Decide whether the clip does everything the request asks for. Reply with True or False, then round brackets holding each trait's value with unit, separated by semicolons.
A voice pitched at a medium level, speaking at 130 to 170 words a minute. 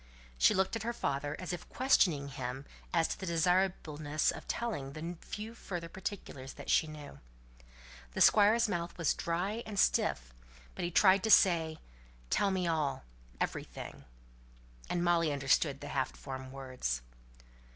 True (165 Hz; 150 wpm)